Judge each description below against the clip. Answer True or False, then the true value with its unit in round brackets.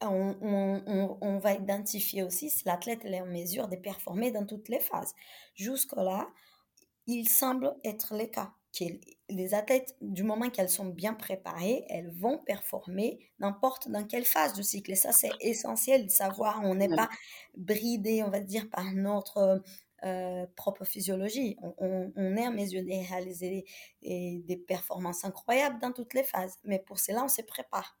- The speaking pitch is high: True (200 Hz)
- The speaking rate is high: False (175 wpm)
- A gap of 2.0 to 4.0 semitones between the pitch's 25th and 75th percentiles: True (3.1 semitones)